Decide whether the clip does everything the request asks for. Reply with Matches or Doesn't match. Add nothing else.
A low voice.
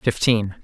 Matches